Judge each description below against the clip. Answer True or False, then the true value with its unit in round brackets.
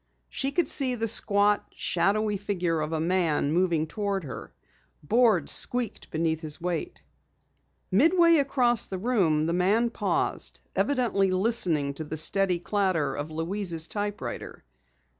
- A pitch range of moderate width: False (5.8 semitones)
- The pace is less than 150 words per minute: True (135 wpm)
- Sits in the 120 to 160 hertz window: False (190 Hz)